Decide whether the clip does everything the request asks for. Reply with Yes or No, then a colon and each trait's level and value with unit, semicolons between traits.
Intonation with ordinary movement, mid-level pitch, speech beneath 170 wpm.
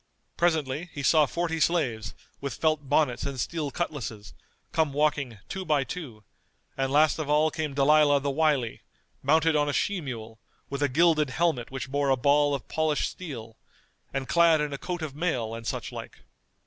No: average, 3.0 semitones; medium, 145 Hz; average, 180 wpm